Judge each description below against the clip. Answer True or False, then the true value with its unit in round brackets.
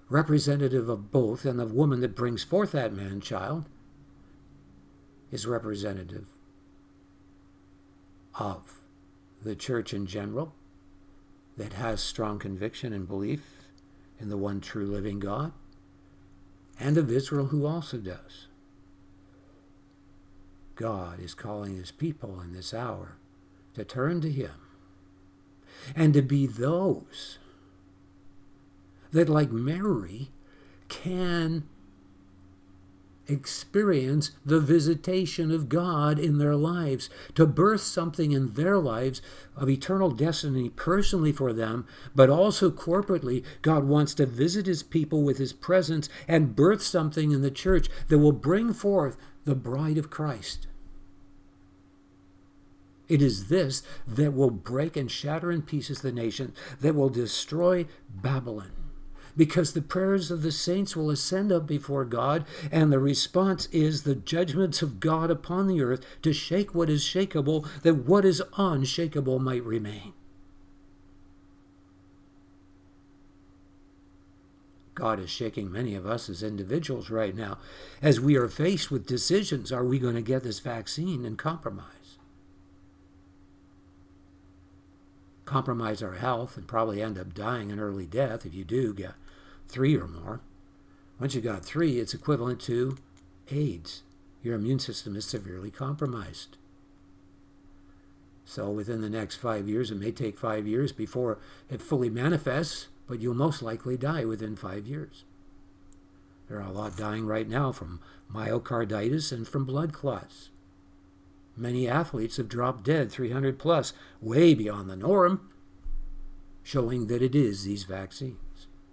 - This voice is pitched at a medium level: False (115 Hz)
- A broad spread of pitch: True (7.5 semitones)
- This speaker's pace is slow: True (130 wpm)